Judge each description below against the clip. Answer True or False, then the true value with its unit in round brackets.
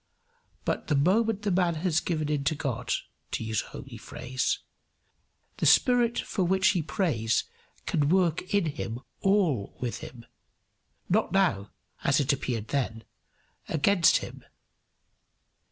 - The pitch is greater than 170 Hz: False (155 Hz)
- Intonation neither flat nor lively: False (6.8 semitones)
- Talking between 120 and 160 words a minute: True (135 wpm)